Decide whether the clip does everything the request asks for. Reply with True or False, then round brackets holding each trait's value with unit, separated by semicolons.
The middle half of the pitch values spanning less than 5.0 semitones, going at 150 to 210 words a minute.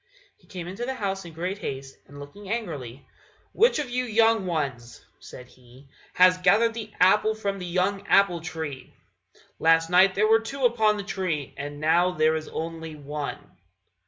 False (5.5 semitones; 175 wpm)